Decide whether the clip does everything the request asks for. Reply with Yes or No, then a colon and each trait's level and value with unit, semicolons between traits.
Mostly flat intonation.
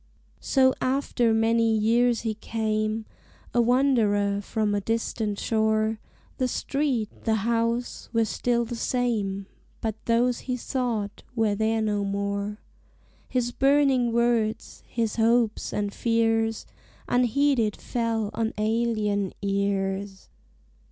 Yes: narrow, 2.1 semitones